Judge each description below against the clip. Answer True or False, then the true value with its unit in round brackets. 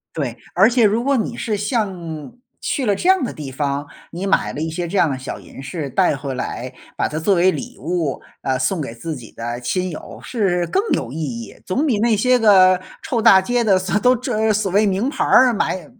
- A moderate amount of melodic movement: False (6.6 semitones)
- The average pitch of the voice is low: False (185 Hz)